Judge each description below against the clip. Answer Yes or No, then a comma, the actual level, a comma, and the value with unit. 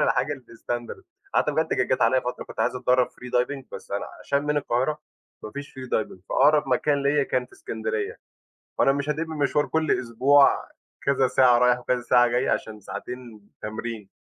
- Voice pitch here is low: Yes, low, 125 Hz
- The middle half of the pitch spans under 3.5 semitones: Yes, average, 2.9 semitones